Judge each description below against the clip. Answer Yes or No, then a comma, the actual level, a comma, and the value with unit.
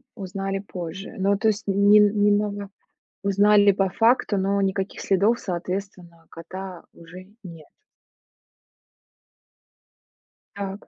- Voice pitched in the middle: No, high, 195 Hz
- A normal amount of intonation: No, narrow, 1.6 semitones